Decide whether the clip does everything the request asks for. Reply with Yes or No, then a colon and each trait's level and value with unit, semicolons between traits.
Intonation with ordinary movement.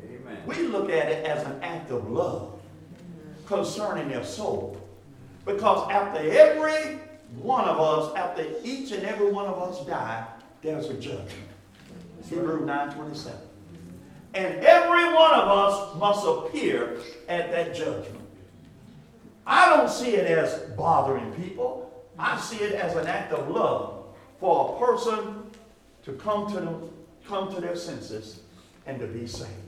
No: wide, 7.9 semitones